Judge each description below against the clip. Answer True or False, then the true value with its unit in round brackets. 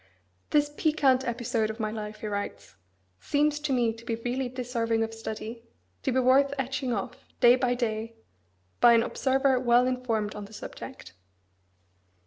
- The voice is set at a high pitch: True (240 Hz)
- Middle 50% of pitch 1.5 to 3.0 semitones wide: True (2.7 semitones)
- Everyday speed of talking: True (160 wpm)